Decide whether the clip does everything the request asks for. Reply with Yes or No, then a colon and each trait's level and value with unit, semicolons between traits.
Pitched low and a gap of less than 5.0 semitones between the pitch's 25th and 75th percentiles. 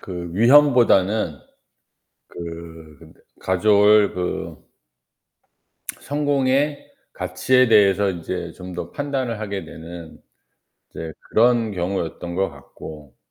No: very low, 95 Hz; wide, 5.6 semitones